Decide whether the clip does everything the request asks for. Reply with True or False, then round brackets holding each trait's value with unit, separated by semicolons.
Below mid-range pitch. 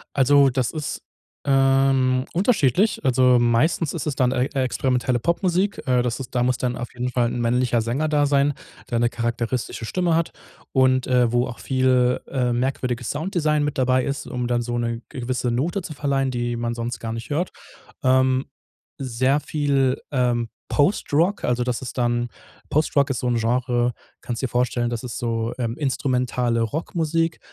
True (130 Hz)